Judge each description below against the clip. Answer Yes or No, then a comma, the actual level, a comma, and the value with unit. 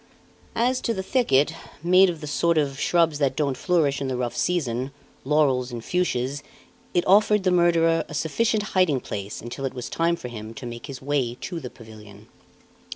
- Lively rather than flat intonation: Yes, wide, 5.7 semitones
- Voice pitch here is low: No, medium, 145 Hz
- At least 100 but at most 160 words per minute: No, average, 190 wpm